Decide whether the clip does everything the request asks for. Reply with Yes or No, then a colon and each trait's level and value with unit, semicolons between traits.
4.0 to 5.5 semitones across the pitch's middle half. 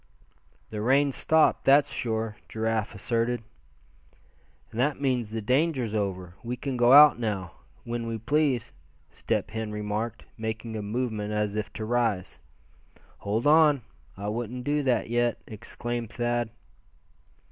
No: average, 2.8 semitones